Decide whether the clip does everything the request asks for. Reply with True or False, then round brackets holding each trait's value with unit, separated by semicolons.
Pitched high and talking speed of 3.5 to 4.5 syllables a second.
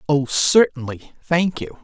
False (145 Hz; 3.9 syllables/s)